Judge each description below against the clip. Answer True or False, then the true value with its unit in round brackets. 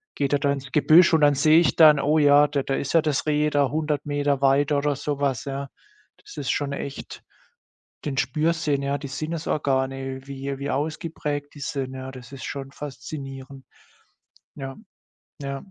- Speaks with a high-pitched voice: False (140 Hz)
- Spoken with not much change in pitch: True (1.6 semitones)